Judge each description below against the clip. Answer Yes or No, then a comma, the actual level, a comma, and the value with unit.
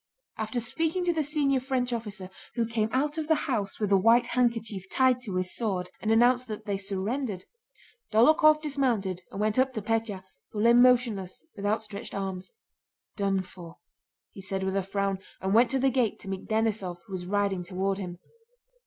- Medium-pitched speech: No, high, 220 Hz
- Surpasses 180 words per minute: Yes, average, 190 wpm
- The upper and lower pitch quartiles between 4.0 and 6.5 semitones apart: Yes, average, 4.4 semitones